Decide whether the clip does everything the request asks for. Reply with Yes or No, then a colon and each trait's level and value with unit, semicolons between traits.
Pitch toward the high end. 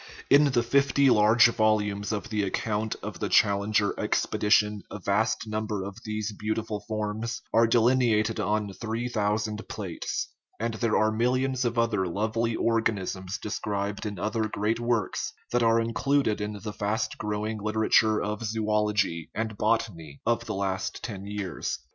No: low, 110 Hz